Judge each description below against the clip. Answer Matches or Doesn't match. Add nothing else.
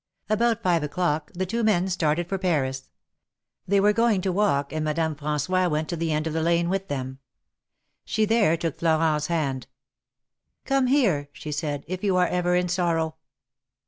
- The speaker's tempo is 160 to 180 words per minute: Matches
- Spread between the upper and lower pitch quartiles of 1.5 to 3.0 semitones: Doesn't match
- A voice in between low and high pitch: Matches